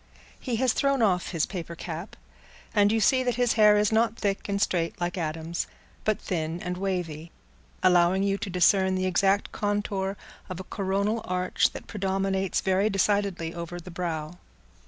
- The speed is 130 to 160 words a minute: No, average, 170 wpm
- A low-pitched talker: No, high, 190 Hz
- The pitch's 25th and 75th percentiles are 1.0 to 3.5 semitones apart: Yes, average, 2.7 semitones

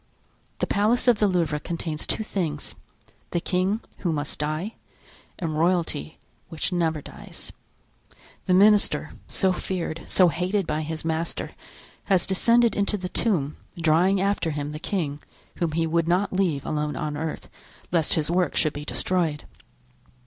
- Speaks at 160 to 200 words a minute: No, average, 150 wpm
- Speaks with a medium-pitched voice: Yes, medium, 170 Hz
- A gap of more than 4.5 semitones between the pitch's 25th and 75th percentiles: No, average, 3.7 semitones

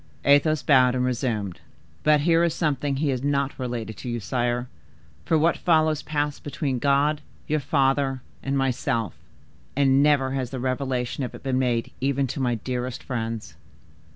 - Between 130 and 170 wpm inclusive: Yes, average, 165 wpm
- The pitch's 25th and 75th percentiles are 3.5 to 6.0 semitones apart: No, narrow, 2.5 semitones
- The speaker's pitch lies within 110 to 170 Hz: Yes, low, 135 Hz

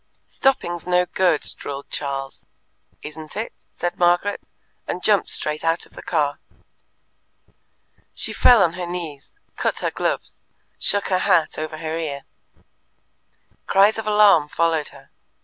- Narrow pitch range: No, average, 3.8 semitones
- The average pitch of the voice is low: No, medium, 170 Hz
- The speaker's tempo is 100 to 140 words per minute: Yes, slow, 135 wpm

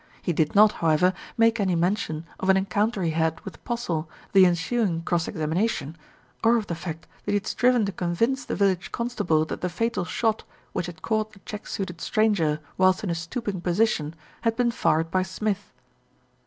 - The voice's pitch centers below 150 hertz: No, medium, 185 Hz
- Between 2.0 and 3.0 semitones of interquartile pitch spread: No, average, 4.7 semitones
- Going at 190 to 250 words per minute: Yes, average, 195 wpm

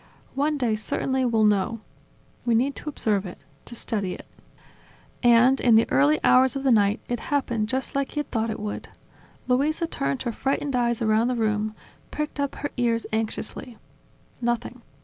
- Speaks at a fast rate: No, average, 175 wpm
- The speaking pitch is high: Yes, high, 235 Hz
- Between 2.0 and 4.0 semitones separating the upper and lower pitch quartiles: Yes, average, 3.5 semitones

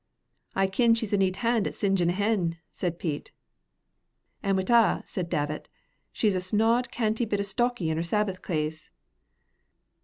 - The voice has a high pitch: Yes, high, 195 Hz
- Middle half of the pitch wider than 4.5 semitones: No, average, 4.2 semitones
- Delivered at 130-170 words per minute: Yes, average, 160 wpm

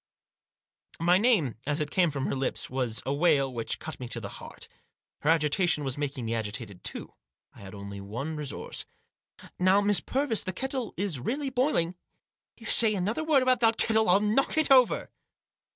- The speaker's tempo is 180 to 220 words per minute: Yes, average, 190 wpm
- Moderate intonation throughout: No, wide, 9.0 semitones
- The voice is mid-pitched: Yes, medium, 170 Hz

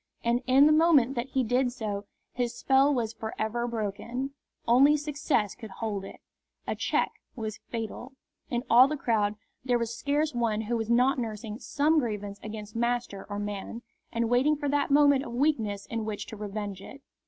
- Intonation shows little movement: No, average, 3.9 semitones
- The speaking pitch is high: Yes, high, 235 Hz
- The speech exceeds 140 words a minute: Yes, average, 185 wpm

